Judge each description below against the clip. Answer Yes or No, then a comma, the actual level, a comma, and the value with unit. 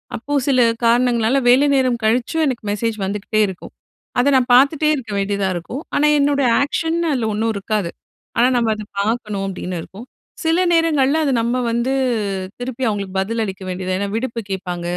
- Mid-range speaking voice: No, high, 235 Hz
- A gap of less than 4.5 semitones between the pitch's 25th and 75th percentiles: No, average, 4.8 semitones